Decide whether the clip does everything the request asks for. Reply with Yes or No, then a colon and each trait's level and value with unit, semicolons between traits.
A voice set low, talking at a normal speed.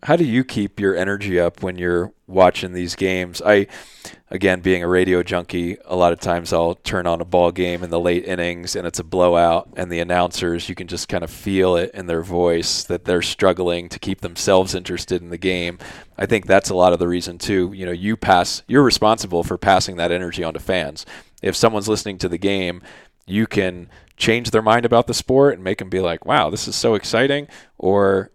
No: very low, 90 Hz; fast, 220 wpm